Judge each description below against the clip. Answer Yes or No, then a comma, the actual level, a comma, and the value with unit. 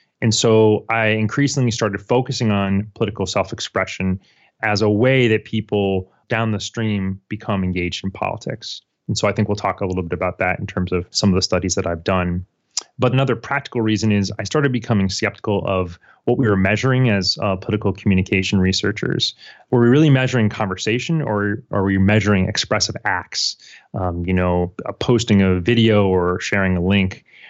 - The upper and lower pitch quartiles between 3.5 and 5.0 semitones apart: No, average, 3.1 semitones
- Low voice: Yes, low, 105 Hz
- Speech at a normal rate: Yes, average, 180 wpm